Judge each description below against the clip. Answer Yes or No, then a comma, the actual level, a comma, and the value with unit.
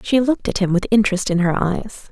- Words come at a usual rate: No, fast, 255 wpm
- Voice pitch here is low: No, high, 200 Hz